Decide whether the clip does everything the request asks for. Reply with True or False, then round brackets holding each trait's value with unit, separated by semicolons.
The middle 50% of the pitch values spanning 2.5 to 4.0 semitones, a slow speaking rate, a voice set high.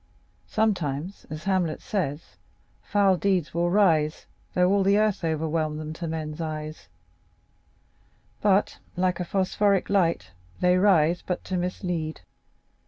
False (3.6 semitones; 125 wpm; 175 Hz)